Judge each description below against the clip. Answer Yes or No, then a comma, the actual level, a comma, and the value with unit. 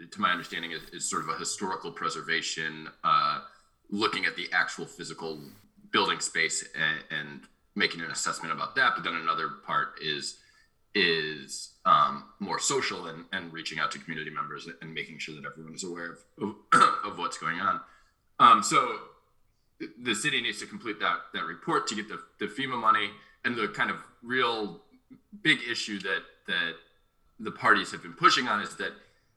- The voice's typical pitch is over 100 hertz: No, very low, 85 Hz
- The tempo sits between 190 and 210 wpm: No, average, 175 wpm